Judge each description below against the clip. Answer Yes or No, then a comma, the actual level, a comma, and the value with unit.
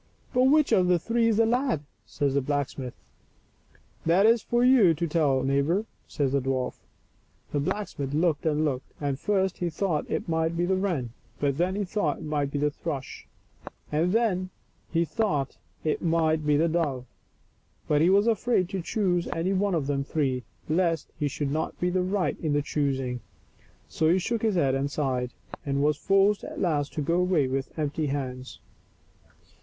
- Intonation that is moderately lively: Yes, average, 4.9 semitones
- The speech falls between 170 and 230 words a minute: Yes, average, 190 wpm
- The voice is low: No, medium, 160 Hz